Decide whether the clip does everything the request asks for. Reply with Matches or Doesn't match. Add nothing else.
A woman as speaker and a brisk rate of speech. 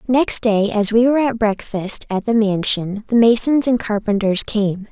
Doesn't match